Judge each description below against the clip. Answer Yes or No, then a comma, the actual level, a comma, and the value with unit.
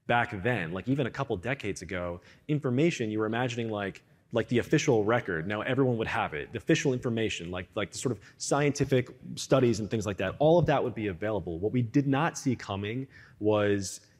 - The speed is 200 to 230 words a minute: Yes, fast, 205 wpm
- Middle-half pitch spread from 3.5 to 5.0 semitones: Yes, average, 4.6 semitones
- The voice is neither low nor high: No, low, 120 Hz